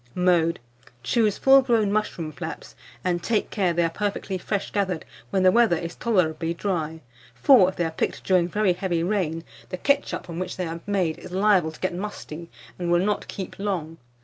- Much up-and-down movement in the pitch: No, average, 3.4 semitones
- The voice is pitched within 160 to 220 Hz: Yes, medium, 185 Hz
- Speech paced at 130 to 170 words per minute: No, average, 195 wpm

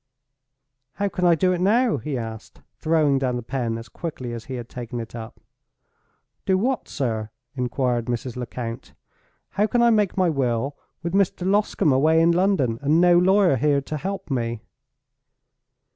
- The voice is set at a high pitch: No, medium, 145 Hz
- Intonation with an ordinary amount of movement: No, wide, 7.2 semitones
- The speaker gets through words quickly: No, average, 170 wpm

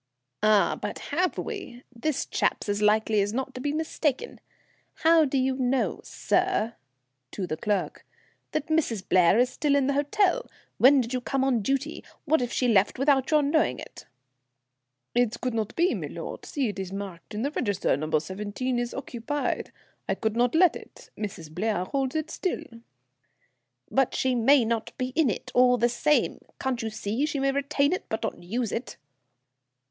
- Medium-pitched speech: No, very high, 250 Hz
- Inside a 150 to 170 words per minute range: No, average, 180 wpm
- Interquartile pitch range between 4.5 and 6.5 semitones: Yes, average, 4.9 semitones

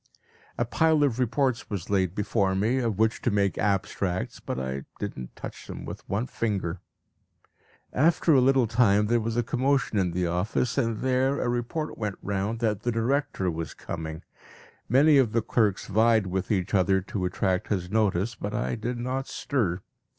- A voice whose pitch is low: Yes, low, 110 Hz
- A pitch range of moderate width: Yes, average, 4.4 semitones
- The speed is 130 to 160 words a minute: No, average, 180 wpm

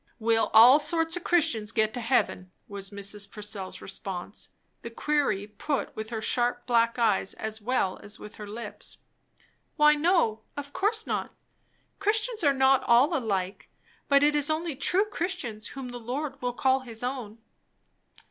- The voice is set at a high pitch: Yes, high, 245 Hz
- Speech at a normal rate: Yes, average, 160 wpm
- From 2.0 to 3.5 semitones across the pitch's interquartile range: No, wide, 5.4 semitones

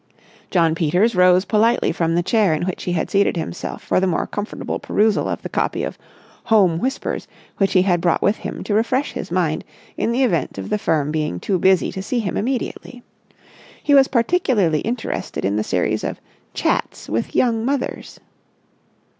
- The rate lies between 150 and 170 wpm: No, average, 185 wpm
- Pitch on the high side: Yes, high, 195 Hz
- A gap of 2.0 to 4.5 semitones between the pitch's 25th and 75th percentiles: No, wide, 5.4 semitones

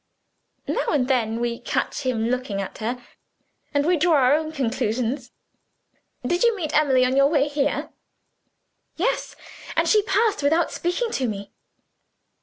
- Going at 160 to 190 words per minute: No, average, 150 wpm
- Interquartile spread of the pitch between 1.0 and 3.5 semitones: No, average, 4.5 semitones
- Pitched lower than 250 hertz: No, very high, 275 Hz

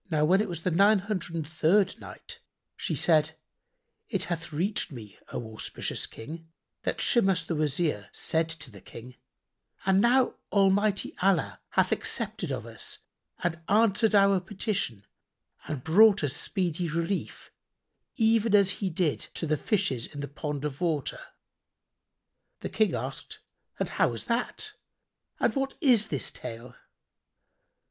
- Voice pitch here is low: No, medium, 175 Hz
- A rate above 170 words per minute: No, average, 145 wpm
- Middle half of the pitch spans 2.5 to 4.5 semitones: No, average, 5.1 semitones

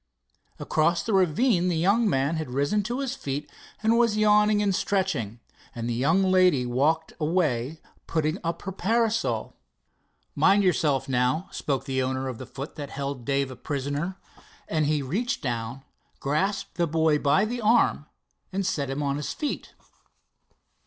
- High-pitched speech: No, medium, 160 Hz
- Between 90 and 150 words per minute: No, average, 160 wpm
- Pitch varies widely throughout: Yes, wide, 6.2 semitones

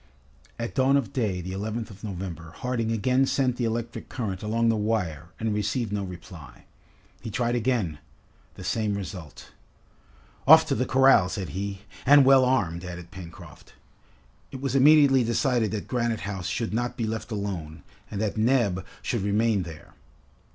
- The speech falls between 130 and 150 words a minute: No, average, 165 wpm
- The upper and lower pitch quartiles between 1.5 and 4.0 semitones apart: No, average, 4.4 semitones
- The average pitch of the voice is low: Yes, low, 110 Hz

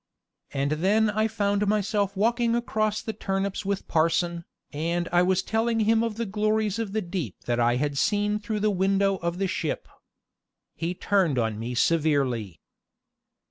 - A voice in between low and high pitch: No, high, 195 Hz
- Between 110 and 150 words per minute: No, average, 165 wpm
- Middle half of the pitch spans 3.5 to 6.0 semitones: Yes, average, 4.3 semitones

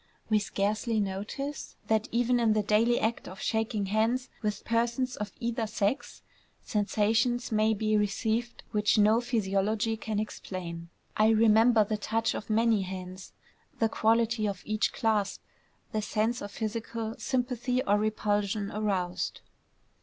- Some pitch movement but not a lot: No, narrow, 1.9 semitones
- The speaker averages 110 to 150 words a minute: Yes, average, 140 wpm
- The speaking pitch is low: No, high, 215 Hz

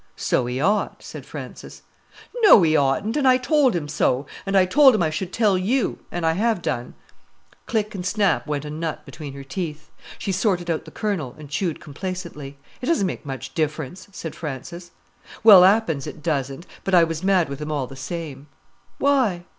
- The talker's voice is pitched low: No, medium, 170 Hz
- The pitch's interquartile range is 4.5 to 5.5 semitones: Yes, average, 5.1 semitones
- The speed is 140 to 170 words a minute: No, average, 190 wpm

